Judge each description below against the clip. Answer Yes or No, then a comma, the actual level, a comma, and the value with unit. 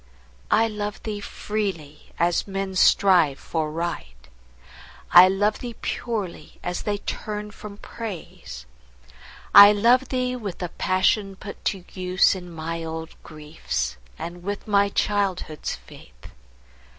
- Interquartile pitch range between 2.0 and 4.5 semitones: Yes, average, 3.8 semitones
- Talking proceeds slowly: Yes, slow, 125 wpm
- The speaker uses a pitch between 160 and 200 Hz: Yes, high, 190 Hz